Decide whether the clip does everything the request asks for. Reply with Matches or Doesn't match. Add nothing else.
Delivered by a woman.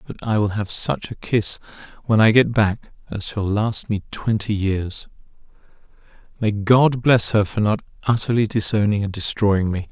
Doesn't match